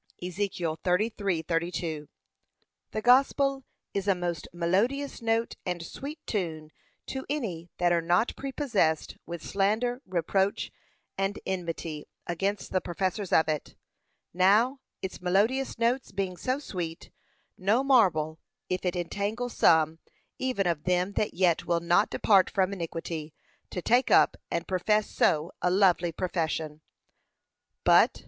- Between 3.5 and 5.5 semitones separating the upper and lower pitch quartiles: Yes, average, 4.3 semitones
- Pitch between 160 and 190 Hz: Yes, medium, 185 Hz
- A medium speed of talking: No, slow, 130 wpm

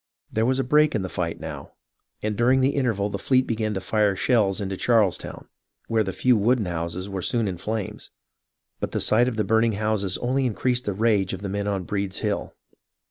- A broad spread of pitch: No, average, 3.5 semitones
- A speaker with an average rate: No, fast, 210 wpm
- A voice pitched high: No, low, 105 Hz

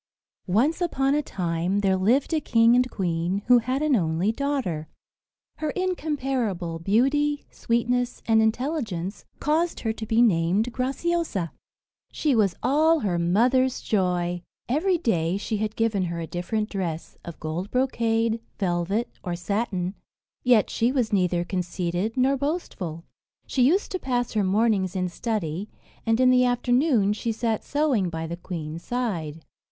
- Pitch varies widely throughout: Yes, wide, 6.2 semitones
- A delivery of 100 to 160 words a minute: Yes, average, 150 wpm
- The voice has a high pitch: Yes, high, 220 Hz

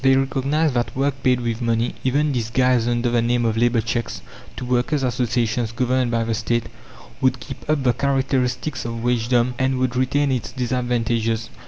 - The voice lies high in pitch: No, low, 125 Hz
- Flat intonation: Yes, narrow, 1.9 semitones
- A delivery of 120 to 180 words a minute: Yes, average, 175 wpm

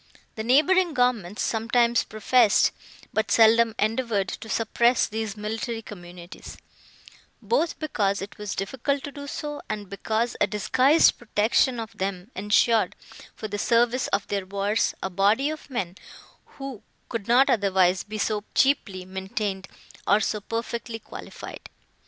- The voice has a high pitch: Yes, high, 220 Hz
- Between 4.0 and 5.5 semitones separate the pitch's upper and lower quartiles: No, average, 3.4 semitones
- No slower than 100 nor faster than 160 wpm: Yes, average, 140 wpm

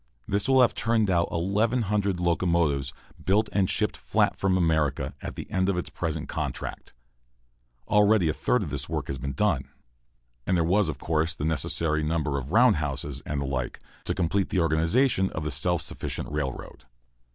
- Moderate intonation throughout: Yes, average, 4.7 semitones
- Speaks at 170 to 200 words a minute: Yes, average, 175 wpm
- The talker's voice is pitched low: Yes, very low, 85 Hz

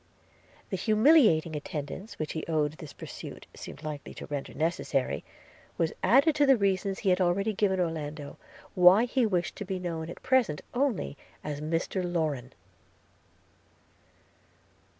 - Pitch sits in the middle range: Yes, medium, 175 Hz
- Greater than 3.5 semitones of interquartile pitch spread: Yes, average, 5.0 semitones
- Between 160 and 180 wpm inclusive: No, average, 140 wpm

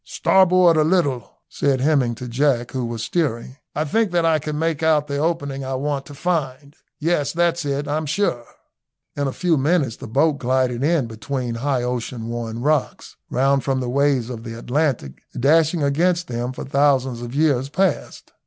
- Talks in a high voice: No, medium, 140 Hz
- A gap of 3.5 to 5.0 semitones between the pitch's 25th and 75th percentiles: Yes, average, 4.0 semitones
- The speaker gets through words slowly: No, average, 180 wpm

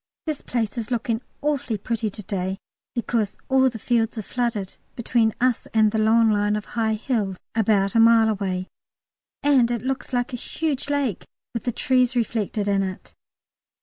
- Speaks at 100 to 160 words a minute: No, average, 175 wpm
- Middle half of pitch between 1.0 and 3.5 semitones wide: Yes, average, 2.8 semitones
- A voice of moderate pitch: No, high, 225 Hz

